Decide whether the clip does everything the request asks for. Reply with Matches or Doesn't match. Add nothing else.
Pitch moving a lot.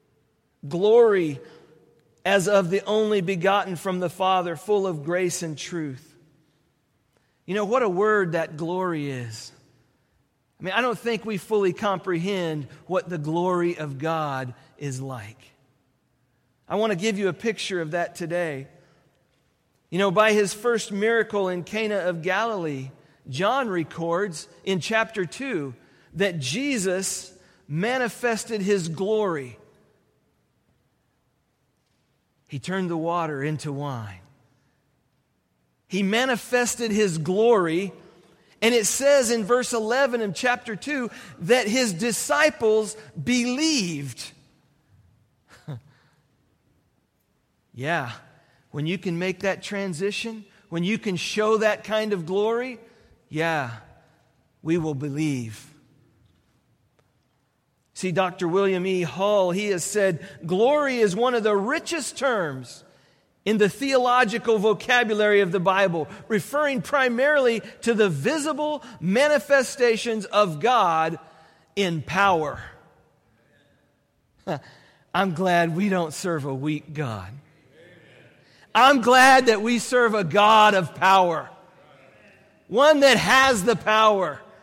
Matches